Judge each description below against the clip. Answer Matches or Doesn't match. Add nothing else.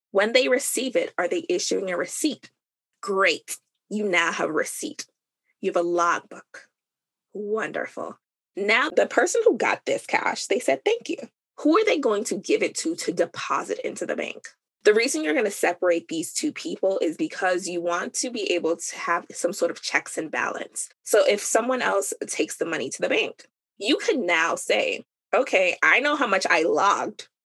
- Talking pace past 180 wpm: Matches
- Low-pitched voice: Doesn't match